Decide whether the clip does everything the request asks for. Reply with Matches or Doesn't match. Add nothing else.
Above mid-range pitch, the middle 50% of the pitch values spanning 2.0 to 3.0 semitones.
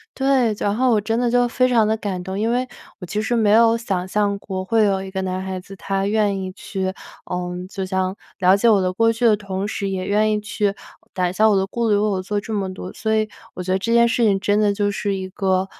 Matches